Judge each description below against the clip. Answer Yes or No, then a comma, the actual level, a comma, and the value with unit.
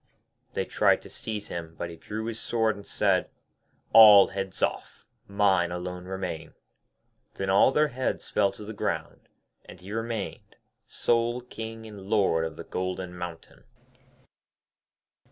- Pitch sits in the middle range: No, low, 100 Hz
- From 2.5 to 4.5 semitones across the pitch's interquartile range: Yes, average, 3.6 semitones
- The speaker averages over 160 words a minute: No, average, 145 wpm